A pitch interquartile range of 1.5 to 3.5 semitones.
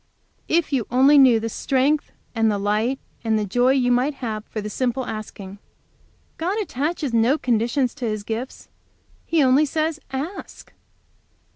No: average, 4.3 semitones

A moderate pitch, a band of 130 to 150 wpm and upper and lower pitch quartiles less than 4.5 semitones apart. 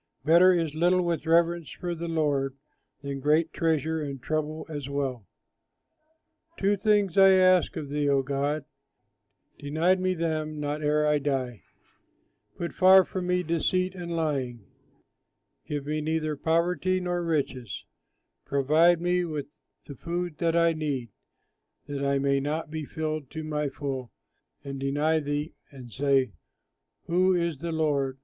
Yes: medium, 155 Hz; average, 145 wpm; average, 3.3 semitones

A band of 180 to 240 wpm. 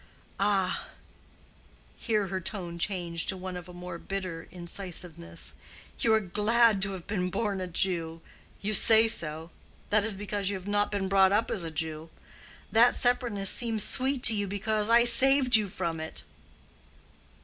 No: average, 160 wpm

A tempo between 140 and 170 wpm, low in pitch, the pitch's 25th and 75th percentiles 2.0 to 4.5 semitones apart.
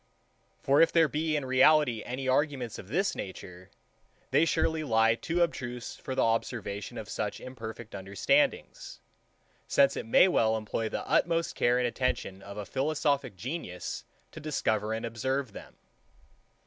No: average, 150 wpm; low, 130 Hz; wide, 5.6 semitones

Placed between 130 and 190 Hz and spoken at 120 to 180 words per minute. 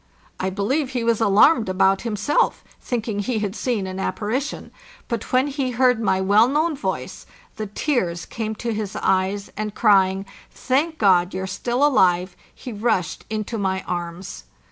No: high, 215 Hz; average, 165 wpm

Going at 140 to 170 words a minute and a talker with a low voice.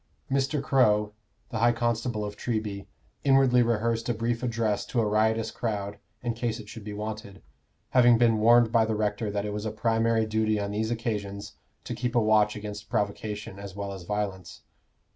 No: average, 185 wpm; low, 110 Hz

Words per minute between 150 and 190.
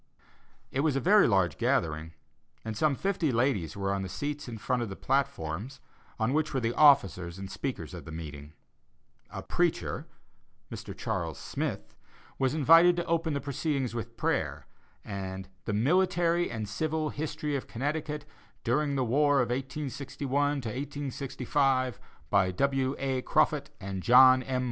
Yes: average, 155 wpm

